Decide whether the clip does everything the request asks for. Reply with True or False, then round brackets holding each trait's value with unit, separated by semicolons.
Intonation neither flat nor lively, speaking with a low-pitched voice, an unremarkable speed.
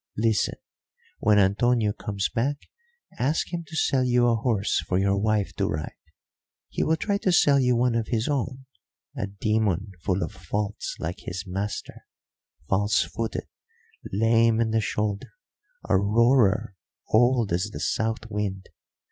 True (3.4 semitones; 110 Hz; 150 wpm)